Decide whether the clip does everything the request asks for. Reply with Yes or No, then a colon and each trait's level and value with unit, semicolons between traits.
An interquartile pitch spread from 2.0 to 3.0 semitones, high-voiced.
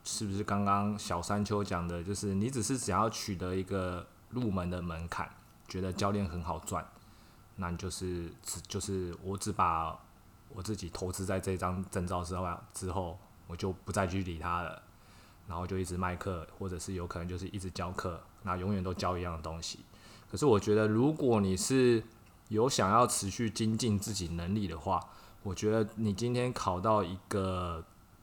No: average, 2.7 semitones; very low, 95 Hz